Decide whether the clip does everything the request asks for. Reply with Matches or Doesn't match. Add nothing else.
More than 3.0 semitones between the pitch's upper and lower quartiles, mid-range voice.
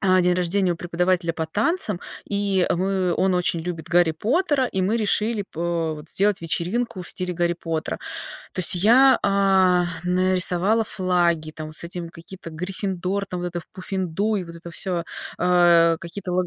Doesn't match